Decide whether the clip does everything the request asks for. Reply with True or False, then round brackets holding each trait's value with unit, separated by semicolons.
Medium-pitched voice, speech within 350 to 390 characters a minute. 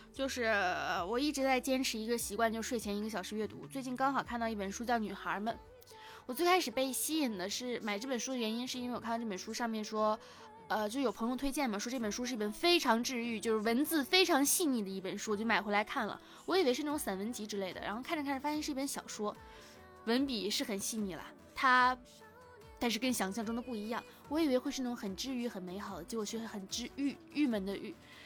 False (235 Hz; 355 characters per minute)